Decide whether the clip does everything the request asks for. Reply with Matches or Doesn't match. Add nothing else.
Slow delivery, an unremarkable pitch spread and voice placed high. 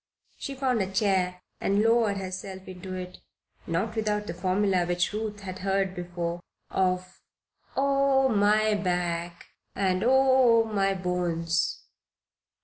Matches